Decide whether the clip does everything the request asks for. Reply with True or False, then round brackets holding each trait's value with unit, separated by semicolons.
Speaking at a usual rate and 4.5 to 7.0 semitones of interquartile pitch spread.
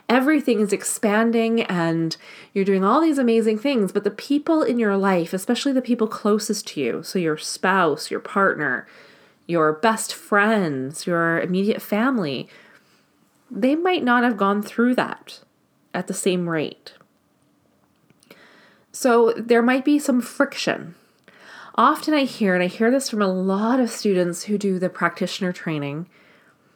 True (150 wpm; 4.8 semitones)